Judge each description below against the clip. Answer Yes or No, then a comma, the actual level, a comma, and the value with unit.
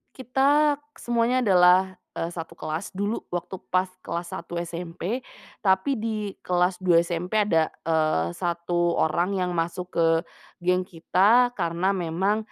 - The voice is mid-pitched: Yes, medium, 180 Hz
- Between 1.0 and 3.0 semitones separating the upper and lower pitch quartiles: No, average, 3.6 semitones